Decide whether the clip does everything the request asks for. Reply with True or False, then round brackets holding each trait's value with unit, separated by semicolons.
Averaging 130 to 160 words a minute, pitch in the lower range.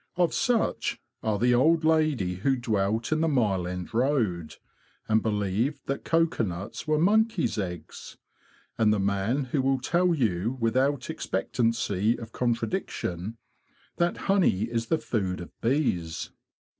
True (135 wpm; 115 Hz)